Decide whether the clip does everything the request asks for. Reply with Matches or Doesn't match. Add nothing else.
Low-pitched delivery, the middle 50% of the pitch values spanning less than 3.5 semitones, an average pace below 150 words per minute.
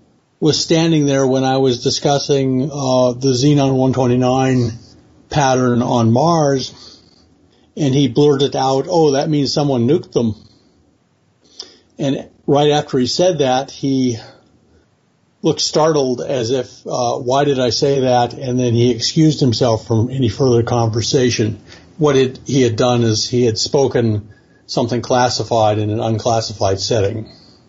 Matches